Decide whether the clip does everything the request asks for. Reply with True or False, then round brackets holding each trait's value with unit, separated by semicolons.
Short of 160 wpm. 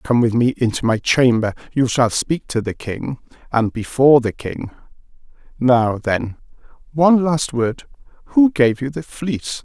True (150 wpm)